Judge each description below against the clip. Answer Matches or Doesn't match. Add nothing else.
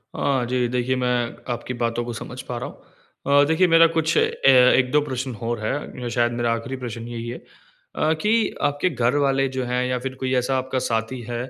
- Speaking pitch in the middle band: Doesn't match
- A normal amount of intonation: Doesn't match